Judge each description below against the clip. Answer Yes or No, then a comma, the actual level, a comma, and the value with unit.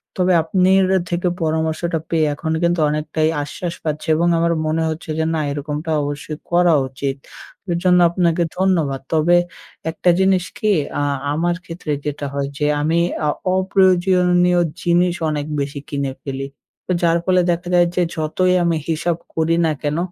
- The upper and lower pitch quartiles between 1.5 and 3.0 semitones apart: Yes, narrow, 2.6 semitones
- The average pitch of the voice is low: No, medium, 165 Hz